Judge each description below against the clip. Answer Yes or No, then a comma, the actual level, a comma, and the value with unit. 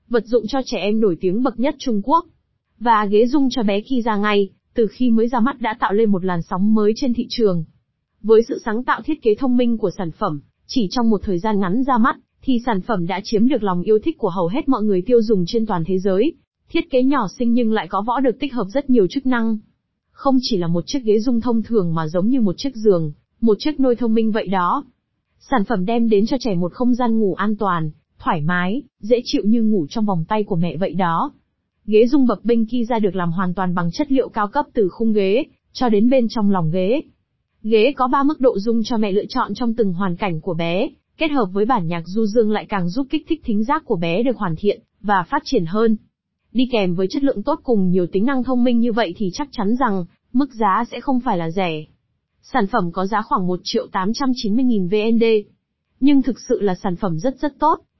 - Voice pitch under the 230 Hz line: Yes, high, 220 Hz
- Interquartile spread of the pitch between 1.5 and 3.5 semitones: No, average, 4.1 semitones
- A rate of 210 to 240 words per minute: No, fast, 250 wpm